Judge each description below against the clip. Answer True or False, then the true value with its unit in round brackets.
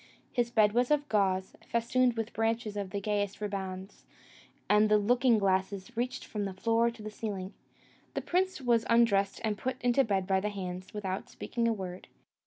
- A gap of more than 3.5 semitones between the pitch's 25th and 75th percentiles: False (3.2 semitones)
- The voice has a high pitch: True (210 Hz)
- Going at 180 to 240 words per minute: True (185 wpm)